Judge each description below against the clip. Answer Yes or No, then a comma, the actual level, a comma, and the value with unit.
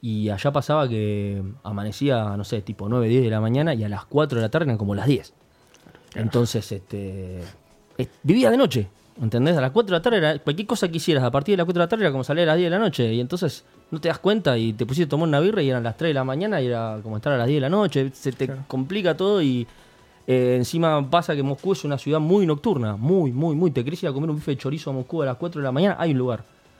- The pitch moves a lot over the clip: Yes, wide, 6.1 semitones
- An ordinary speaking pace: No, fast, 280 wpm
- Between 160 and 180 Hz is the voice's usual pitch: No, medium, 140 Hz